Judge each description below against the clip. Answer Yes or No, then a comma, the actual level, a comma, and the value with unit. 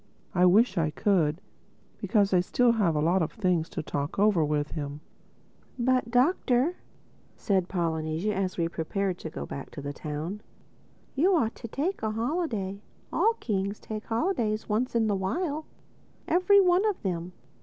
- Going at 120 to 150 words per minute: No, average, 160 wpm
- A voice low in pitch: No, high, 200 Hz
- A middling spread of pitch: No, wide, 6.6 semitones